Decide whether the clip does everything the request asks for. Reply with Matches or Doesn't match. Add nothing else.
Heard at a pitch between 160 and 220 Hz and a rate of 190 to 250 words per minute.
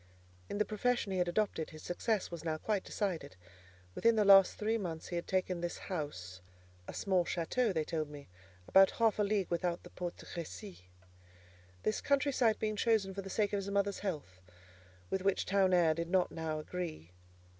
Matches